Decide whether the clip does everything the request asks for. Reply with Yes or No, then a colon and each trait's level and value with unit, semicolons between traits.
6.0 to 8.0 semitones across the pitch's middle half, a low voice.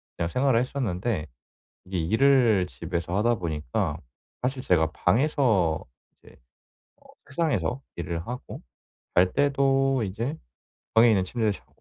Yes: wide, 7.0 semitones; low, 110 Hz